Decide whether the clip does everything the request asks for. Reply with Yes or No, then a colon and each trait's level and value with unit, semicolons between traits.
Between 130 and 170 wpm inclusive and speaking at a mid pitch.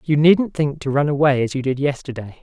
No: fast, 245 wpm; medium, 145 Hz